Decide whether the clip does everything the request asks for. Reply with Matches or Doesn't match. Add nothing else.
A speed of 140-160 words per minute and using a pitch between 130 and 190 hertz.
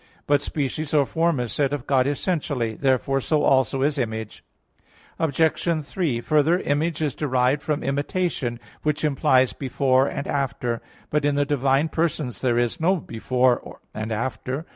Matches